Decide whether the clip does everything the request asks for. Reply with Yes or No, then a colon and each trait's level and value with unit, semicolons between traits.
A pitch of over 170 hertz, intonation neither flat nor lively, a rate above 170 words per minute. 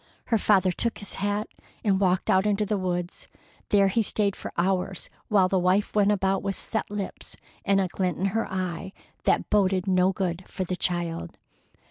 No: high, 190 Hz; narrow, 1.8 semitones; average, 185 wpm